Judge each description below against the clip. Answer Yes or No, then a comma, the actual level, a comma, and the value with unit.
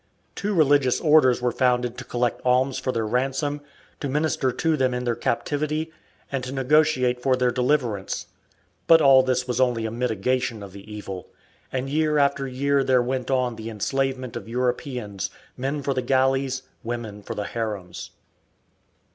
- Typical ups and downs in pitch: No, narrow, 2.3 semitones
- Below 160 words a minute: No, average, 165 wpm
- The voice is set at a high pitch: No, low, 130 Hz